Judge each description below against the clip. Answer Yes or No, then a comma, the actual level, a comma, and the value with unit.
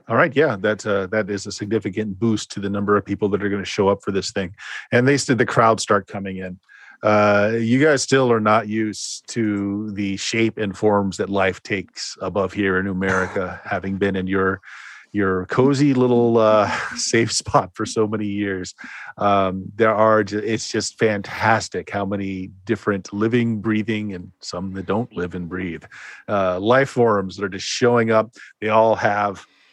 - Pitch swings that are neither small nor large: No, narrow, 2.2 semitones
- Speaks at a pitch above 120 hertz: No, low, 105 Hz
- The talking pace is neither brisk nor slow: Yes, average, 190 wpm